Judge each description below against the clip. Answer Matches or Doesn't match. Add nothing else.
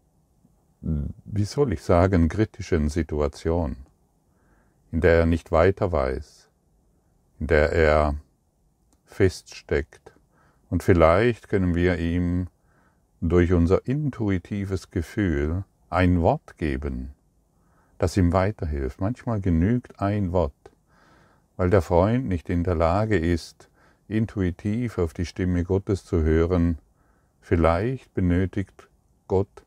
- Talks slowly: Matches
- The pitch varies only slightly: Doesn't match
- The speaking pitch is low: Matches